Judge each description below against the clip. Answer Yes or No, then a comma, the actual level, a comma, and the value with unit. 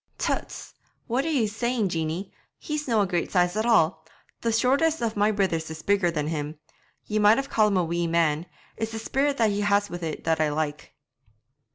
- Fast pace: Yes, fast, 210 wpm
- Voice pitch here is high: Yes, high, 200 Hz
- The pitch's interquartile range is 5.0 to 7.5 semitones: Yes, wide, 5.5 semitones